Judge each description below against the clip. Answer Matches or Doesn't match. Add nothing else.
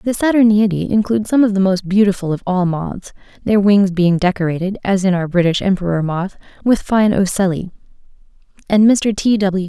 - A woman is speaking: Matches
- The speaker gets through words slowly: Doesn't match